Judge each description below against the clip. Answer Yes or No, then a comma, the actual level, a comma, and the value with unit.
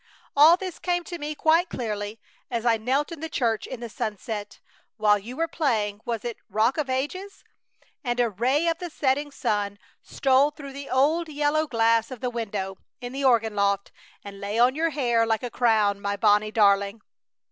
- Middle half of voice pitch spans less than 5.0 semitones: No, wide, 5.5 semitones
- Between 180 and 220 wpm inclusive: Yes, average, 190 wpm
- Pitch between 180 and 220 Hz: No, high, 240 Hz